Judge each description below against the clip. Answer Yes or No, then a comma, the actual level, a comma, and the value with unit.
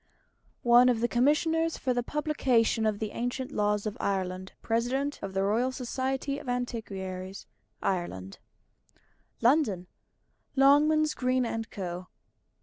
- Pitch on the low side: No, high, 240 Hz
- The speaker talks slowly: Yes, slow, 125 wpm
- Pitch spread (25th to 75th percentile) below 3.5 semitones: No, average, 5.1 semitones